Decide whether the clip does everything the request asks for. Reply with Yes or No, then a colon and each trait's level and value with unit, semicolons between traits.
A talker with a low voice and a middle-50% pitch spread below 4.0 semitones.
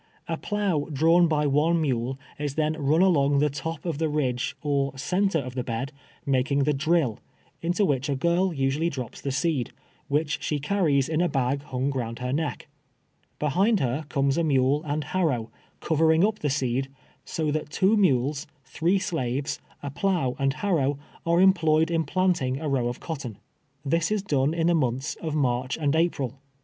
No: medium, 150 Hz; average, 3.6 semitones